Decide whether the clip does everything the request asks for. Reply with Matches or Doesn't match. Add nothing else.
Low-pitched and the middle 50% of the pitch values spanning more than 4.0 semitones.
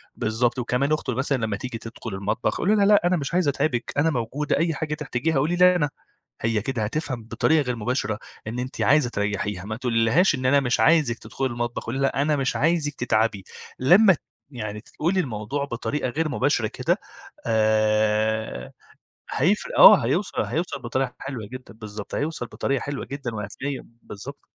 Matches